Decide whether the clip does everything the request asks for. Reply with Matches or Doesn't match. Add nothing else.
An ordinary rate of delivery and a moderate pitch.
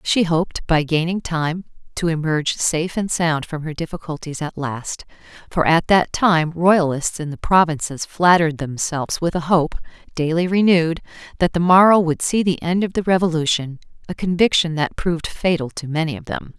Matches